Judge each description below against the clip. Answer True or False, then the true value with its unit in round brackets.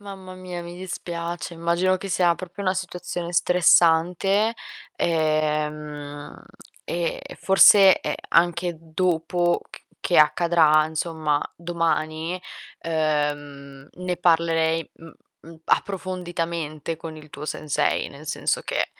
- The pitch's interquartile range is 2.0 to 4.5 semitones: True (2.4 semitones)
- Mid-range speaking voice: True (170 Hz)